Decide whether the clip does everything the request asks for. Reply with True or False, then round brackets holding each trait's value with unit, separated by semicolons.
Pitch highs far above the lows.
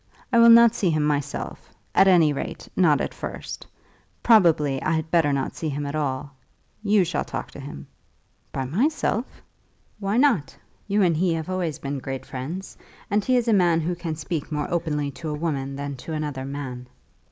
False (4.7 semitones)